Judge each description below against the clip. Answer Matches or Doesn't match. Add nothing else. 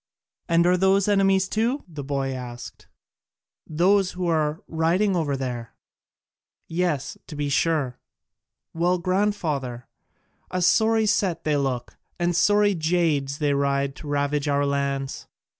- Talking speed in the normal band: Doesn't match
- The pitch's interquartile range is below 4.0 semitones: Doesn't match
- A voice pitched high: Doesn't match